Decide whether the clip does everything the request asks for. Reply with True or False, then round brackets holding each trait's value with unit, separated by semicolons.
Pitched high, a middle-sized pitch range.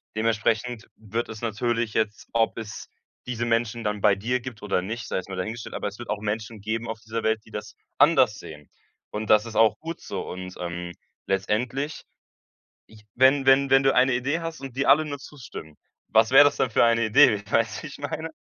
False (115 Hz; 3.4 semitones)